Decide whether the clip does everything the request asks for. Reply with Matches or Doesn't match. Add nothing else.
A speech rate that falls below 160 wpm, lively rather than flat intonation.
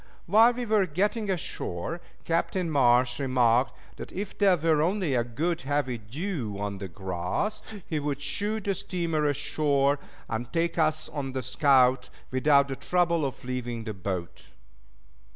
Matches